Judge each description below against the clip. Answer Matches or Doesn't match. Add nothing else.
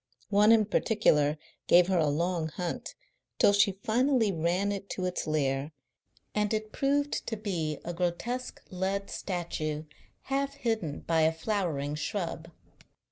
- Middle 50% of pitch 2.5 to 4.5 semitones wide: Doesn't match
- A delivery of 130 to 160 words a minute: Matches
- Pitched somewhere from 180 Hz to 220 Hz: Matches